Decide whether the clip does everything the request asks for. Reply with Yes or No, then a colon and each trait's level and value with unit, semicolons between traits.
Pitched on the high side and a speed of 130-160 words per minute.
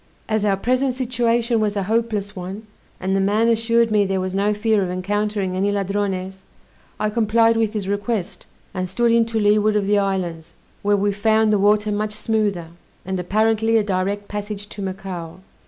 No: high, 205 Hz; average, 185 wpm